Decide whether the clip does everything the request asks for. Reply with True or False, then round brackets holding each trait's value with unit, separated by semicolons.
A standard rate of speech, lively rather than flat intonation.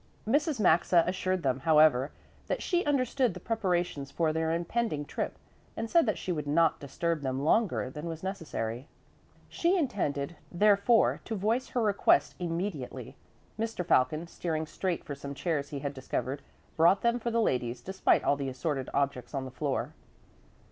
True (165 wpm; 6.7 semitones)